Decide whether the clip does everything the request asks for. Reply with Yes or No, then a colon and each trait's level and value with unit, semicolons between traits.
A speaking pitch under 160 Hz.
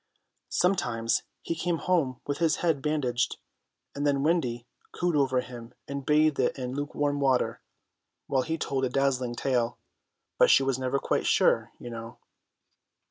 Yes: low, 135 Hz